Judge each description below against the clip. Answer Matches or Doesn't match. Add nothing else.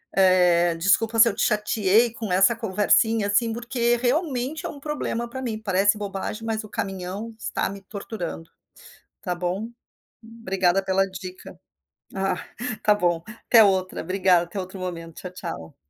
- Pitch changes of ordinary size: Matches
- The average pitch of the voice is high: Matches